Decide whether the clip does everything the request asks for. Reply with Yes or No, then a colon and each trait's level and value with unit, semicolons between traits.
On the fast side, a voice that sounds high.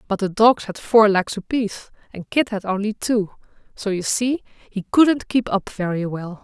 No: average, 195 wpm; high, 210 Hz